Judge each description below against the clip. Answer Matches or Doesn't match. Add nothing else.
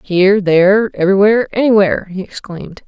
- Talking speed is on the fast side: Doesn't match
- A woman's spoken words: Matches